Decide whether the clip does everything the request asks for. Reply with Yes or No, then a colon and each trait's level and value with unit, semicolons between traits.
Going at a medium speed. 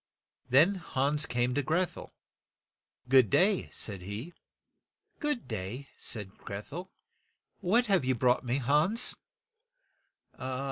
No: slow, 130 wpm